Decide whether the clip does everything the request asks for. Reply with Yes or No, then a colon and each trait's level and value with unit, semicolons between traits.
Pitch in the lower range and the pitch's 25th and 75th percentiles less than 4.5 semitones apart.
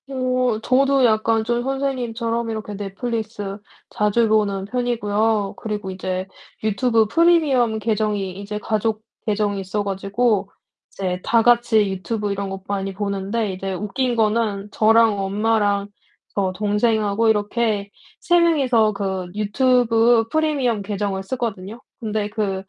No: high, 215 Hz; average, 2.8 semitones